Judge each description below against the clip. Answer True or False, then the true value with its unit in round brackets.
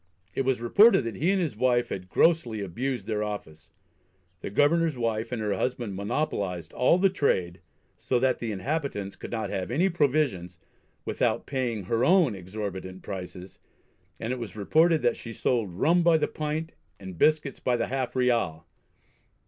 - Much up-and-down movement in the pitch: True (7.0 semitones)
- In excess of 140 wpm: True (170 wpm)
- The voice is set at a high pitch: False (120 Hz)